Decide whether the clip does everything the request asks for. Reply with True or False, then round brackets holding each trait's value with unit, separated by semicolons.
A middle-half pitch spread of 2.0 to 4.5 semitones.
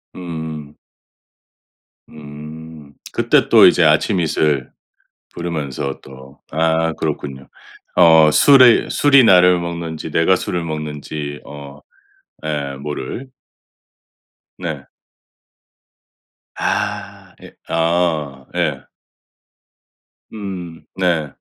True (2.8 semitones)